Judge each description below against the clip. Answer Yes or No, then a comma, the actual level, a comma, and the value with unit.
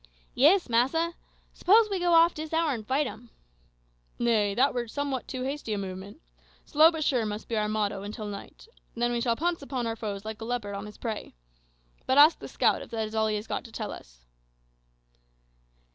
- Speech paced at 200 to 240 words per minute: Yes, fast, 205 wpm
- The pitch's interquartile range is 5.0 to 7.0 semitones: Yes, wide, 5.4 semitones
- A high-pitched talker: Yes, high, 235 Hz